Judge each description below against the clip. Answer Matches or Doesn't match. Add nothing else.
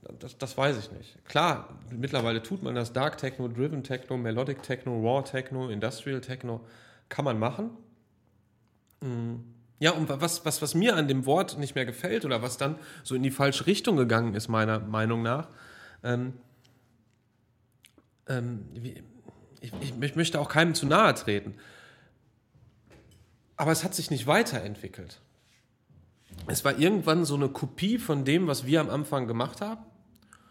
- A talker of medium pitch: Doesn't match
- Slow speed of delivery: Doesn't match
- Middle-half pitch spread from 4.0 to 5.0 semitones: Matches